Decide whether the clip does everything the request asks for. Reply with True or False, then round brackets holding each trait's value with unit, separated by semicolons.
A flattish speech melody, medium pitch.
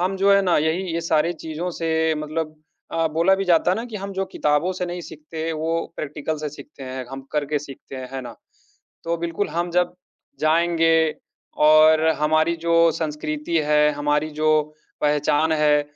True (2.1 semitones; 160 Hz)